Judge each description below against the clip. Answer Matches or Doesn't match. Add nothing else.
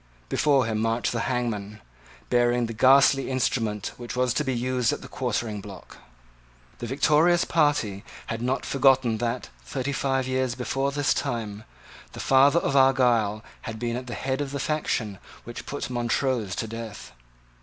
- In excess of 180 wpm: Doesn't match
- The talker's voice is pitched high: Doesn't match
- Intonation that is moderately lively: Matches